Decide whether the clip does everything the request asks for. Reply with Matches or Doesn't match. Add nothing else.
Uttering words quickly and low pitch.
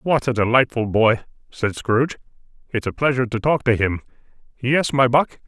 Doesn't match